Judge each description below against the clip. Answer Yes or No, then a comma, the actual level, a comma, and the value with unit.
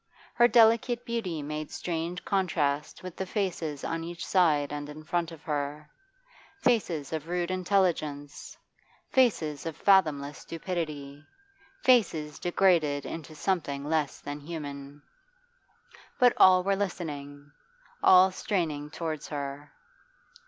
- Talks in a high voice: No, medium, 160 Hz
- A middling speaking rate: No, slow, 115 wpm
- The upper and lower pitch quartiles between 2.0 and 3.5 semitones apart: No, average, 4.1 semitones